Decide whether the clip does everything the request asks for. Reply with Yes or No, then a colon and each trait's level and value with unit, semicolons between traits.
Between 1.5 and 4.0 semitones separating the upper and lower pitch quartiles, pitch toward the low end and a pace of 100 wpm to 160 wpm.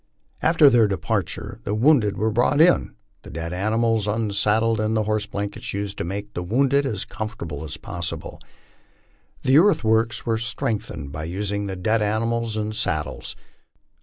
Yes: narrow, 2.4 semitones; low, 110 Hz; average, 155 wpm